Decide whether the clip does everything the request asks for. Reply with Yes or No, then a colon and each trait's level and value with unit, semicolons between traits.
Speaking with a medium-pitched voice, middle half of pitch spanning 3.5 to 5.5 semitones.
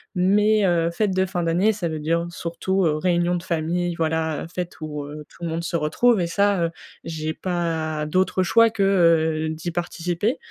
No: medium, 170 Hz; average, 2.7 semitones